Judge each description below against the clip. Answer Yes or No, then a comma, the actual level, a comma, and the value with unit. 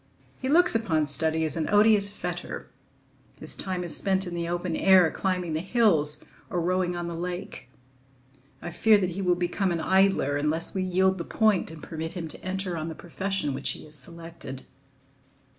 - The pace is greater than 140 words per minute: Yes, average, 190 wpm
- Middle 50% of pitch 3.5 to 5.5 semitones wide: No, average, 2.9 semitones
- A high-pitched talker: No, medium, 175 Hz